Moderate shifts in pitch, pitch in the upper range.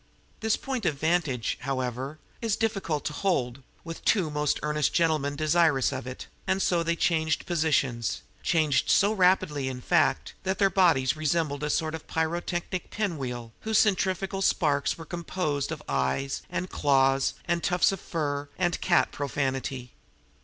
No: average, 4.4 semitones; medium, 155 Hz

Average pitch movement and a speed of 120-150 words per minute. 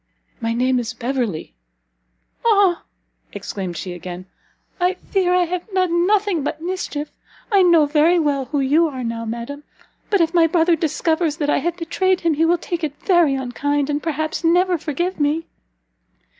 No: average, 4.4 semitones; average, 170 wpm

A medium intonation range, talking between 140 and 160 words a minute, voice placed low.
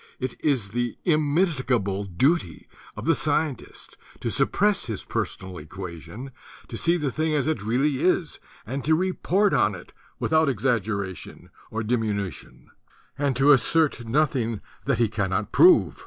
No: wide, 7.0 semitones; average, 150 wpm; low, 130 Hz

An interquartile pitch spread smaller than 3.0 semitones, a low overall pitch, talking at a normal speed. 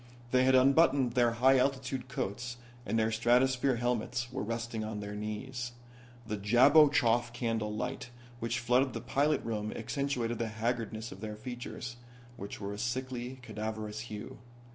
Yes: narrow, 2.6 semitones; low, 120 Hz; average, 150 wpm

